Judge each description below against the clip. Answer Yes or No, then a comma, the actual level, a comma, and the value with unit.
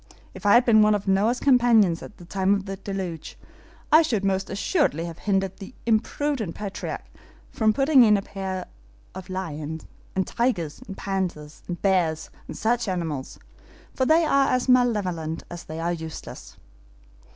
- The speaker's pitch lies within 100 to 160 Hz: No, high, 195 Hz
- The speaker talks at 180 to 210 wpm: No, average, 160 wpm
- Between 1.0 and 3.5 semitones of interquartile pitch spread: No, average, 5.1 semitones